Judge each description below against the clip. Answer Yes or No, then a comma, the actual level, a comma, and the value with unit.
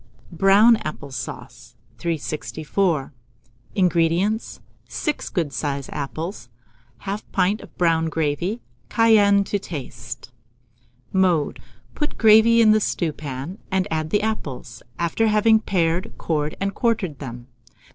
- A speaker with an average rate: No, slow, 115 wpm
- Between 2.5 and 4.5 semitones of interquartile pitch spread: No, wide, 5.6 semitones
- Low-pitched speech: No, medium, 175 Hz